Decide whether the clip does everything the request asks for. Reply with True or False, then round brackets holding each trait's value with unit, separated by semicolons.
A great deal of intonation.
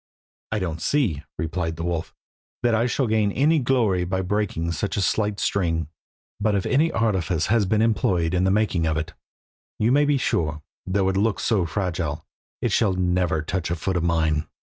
False (4.6 semitones)